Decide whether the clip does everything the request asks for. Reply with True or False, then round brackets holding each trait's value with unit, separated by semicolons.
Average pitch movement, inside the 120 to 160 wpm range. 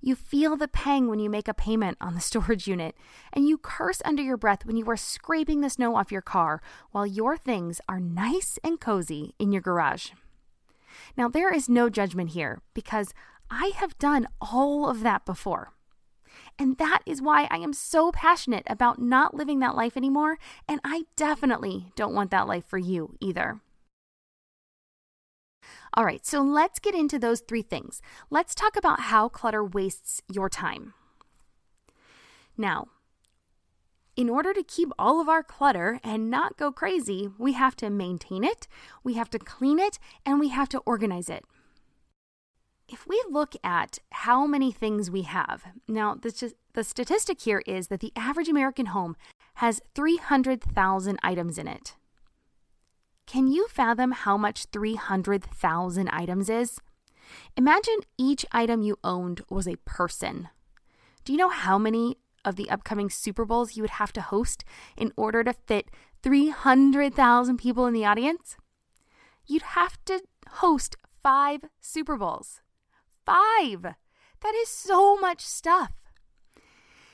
False (6.5 semitones; 155 wpm)